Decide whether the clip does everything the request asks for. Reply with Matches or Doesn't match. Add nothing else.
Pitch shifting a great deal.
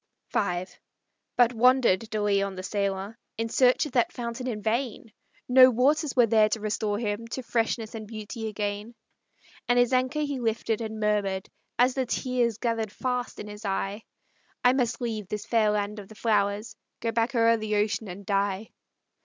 Doesn't match